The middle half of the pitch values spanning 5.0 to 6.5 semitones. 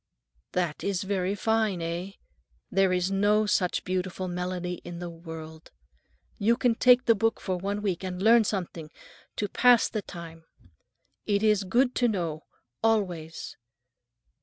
No: average, 3.3 semitones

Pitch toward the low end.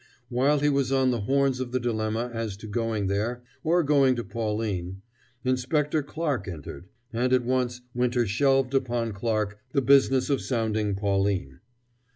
Yes: low, 120 Hz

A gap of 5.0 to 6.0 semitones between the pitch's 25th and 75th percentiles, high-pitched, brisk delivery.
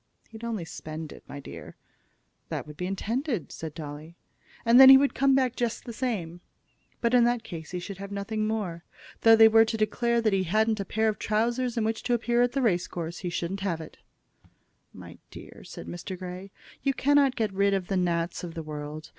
Yes: wide, 5.5 semitones; high, 200 Hz; fast, 215 wpm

